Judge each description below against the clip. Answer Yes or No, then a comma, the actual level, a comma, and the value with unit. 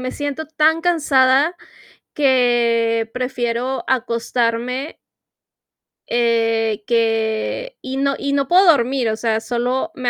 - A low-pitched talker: No, very high, 250 Hz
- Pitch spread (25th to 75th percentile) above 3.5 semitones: No, average, 3.2 semitones